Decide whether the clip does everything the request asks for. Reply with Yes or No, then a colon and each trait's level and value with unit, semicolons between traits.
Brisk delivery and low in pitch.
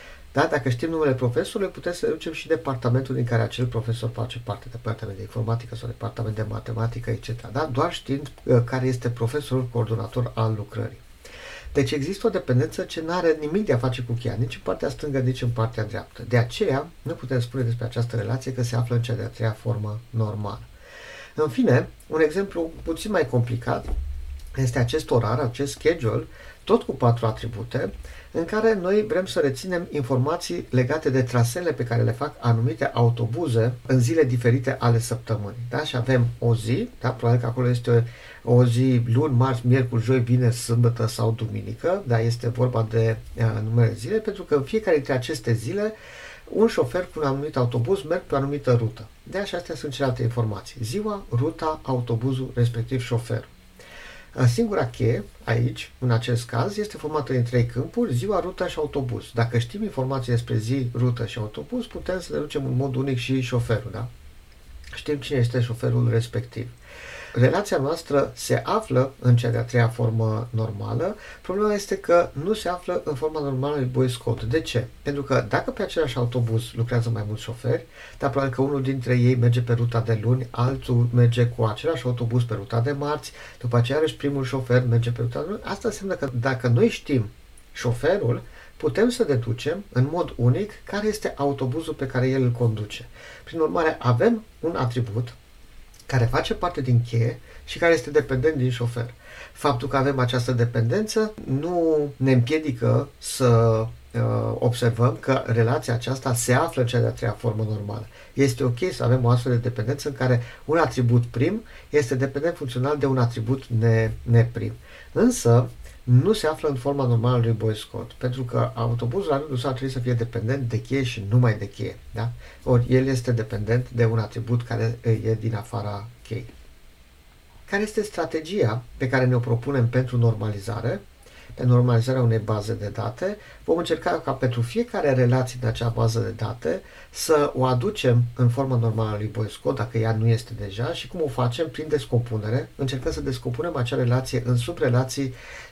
Yes: fast, 180 wpm; low, 125 Hz